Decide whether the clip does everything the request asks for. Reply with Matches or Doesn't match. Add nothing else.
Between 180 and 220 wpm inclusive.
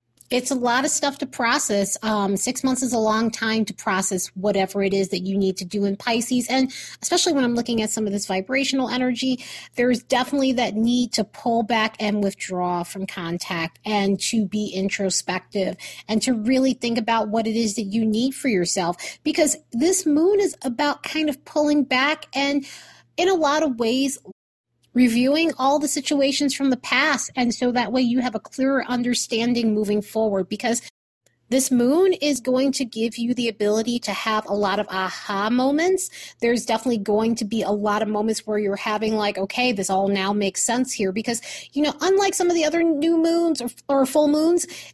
Matches